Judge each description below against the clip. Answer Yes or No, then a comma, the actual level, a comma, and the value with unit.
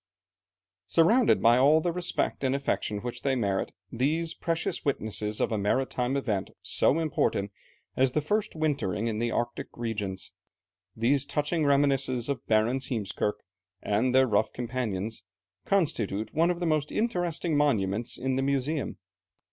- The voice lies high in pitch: No, low, 130 Hz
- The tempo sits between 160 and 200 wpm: No, average, 145 wpm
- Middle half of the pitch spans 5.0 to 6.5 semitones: Yes, average, 5.3 semitones